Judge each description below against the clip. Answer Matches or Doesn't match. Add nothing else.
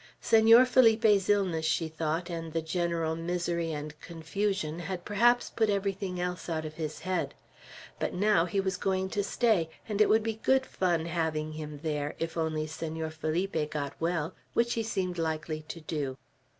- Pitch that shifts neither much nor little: Matches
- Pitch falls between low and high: Matches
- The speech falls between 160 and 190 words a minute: Matches